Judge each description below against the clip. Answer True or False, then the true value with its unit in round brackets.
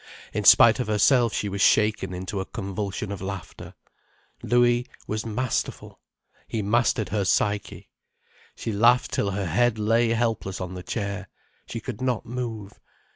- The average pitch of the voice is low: True (105 Hz)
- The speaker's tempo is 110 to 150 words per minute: True (145 wpm)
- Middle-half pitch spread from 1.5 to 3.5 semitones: True (3.0 semitones)